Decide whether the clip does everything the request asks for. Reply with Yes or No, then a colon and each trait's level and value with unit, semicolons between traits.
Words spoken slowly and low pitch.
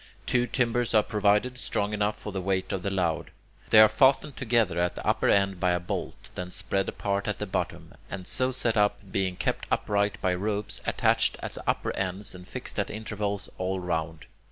No: fast, 205 wpm; low, 100 Hz